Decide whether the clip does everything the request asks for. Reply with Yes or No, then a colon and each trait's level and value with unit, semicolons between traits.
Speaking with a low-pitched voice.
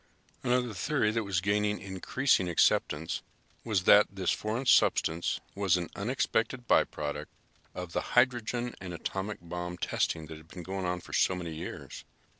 Yes: very low, 95 Hz